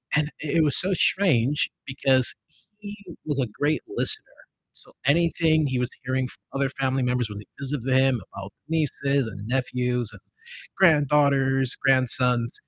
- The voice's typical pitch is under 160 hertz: Yes, low, 135 Hz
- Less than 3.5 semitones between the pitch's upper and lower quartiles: Yes, average, 3.0 semitones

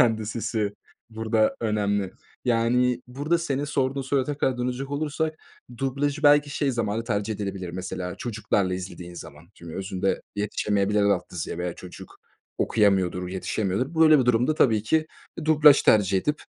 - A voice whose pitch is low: Yes, low, 110 Hz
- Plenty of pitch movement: Yes, wide, 5.9 semitones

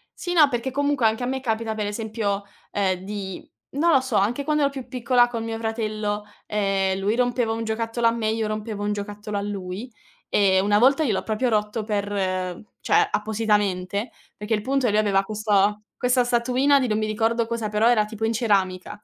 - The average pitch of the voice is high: Yes, high, 220 Hz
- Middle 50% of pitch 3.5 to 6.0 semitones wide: No, average, 2.7 semitones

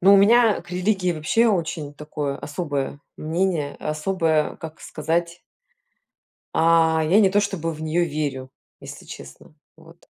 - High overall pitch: No, medium, 165 Hz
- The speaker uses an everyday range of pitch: Yes, average, 3.6 semitones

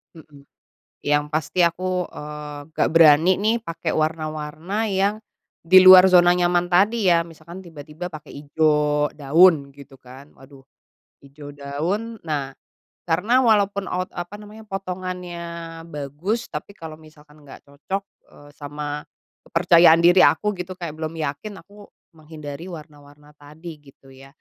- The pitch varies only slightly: No, average, 3.8 semitones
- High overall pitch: No, medium, 165 Hz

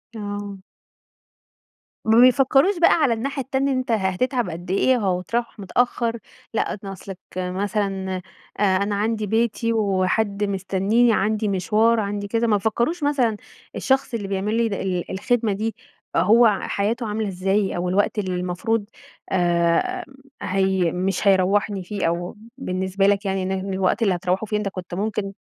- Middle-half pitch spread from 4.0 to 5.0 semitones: No, average, 3.2 semitones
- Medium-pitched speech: No, high, 205 Hz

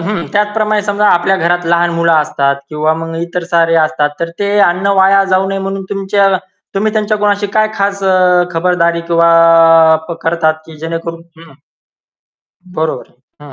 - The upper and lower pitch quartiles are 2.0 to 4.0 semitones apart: Yes, average, 3.1 semitones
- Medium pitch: Yes, medium, 175 Hz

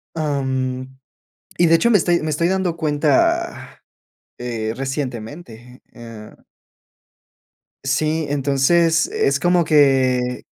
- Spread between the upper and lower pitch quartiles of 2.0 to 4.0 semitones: No, average, 4.4 semitones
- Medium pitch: Yes, medium, 145 Hz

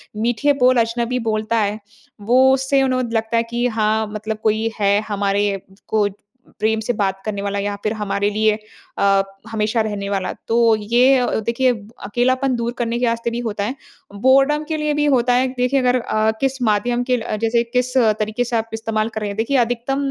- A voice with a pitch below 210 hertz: No, high, 230 Hz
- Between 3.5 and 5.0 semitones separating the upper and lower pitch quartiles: No, average, 2.7 semitones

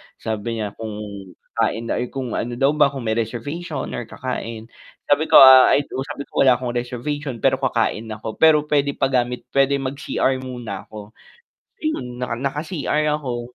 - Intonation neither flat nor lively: Yes, average, 3.2 semitones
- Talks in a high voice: No, low, 130 Hz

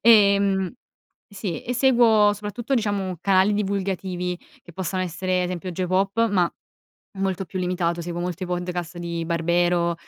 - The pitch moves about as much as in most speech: No, narrow, 2.3 semitones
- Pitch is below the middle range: No, medium, 185 Hz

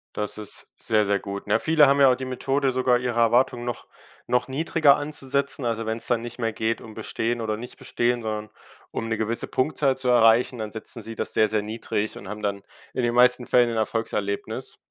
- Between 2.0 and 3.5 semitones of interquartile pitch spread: Yes, average, 2.7 semitones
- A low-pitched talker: Yes, low, 115 Hz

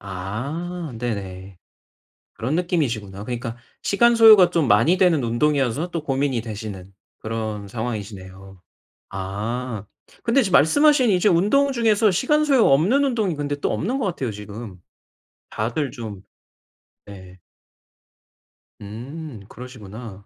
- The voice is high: No, low, 125 Hz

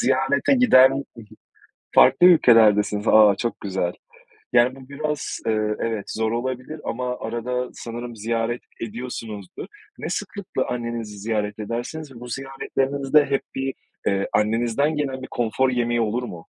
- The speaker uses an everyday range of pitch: Yes, average, 3.2 semitones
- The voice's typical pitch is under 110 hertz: No, low, 120 Hz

